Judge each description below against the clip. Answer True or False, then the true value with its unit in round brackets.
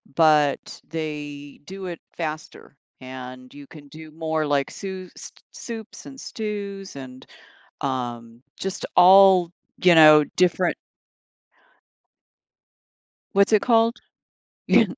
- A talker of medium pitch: True (160 Hz)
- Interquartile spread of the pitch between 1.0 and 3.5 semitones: False (5.2 semitones)